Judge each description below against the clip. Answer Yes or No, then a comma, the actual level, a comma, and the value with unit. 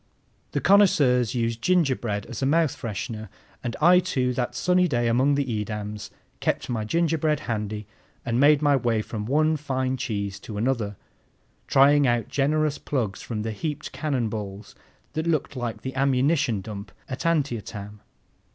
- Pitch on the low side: Yes, low, 125 Hz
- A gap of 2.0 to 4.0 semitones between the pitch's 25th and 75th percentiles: No, average, 5.1 semitones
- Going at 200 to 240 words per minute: No, average, 155 wpm